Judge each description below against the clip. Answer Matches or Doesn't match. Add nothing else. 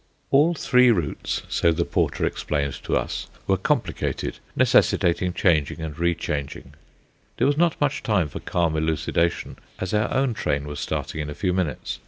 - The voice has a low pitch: Matches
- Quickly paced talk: Doesn't match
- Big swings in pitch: Matches